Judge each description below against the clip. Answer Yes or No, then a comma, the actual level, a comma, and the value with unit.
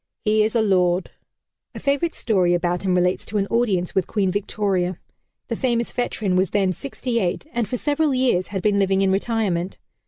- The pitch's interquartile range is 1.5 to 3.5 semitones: No, average, 4.1 semitones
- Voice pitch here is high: Yes, high, 200 Hz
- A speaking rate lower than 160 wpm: No, average, 190 wpm